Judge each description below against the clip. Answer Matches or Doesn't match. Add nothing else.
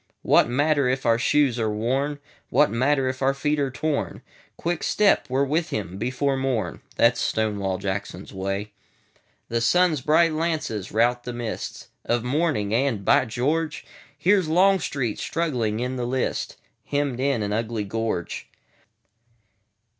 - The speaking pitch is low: Matches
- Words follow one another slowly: Matches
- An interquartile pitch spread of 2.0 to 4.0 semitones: Doesn't match